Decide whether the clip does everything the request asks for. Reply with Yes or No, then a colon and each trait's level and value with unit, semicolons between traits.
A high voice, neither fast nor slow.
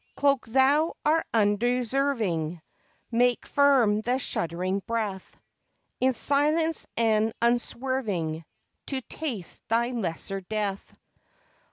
No: high, 230 Hz; slow, 90 wpm